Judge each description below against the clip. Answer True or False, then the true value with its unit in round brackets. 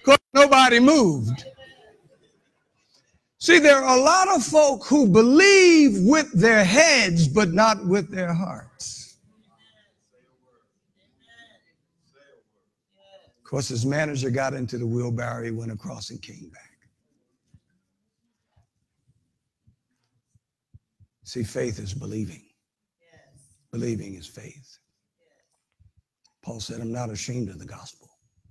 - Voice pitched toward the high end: False (135 Hz)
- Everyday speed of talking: False (105 wpm)